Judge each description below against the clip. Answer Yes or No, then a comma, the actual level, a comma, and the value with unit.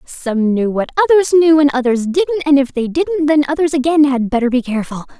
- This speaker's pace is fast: Yes, fast, 220 wpm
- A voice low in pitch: No, very high, 285 Hz